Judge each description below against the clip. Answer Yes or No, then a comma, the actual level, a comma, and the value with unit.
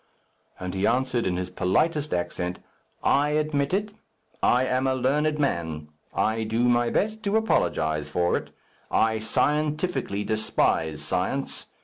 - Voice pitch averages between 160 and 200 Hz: No, low, 120 Hz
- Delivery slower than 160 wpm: Yes, slow, 135 wpm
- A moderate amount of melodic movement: No, wide, 8.5 semitones